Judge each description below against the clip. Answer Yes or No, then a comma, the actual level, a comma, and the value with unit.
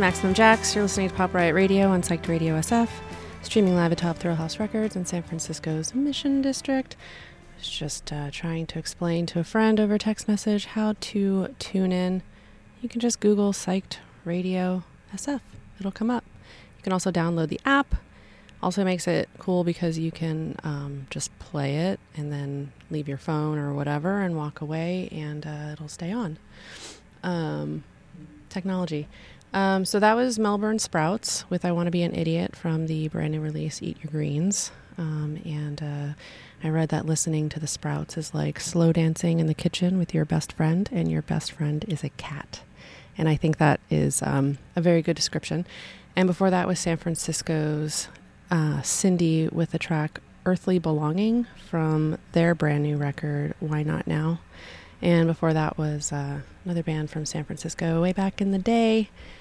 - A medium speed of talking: Yes, average, 180 wpm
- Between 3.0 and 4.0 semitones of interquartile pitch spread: Yes, average, 3.5 semitones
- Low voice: No, medium, 165 Hz